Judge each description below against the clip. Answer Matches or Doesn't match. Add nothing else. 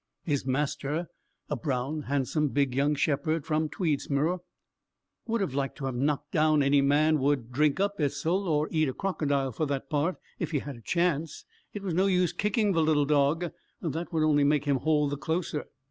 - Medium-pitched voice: Matches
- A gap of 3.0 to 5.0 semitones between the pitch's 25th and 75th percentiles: Doesn't match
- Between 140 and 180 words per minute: Doesn't match